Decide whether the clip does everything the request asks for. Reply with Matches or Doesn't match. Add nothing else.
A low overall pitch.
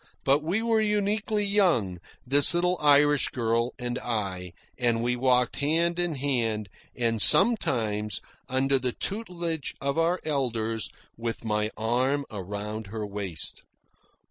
Matches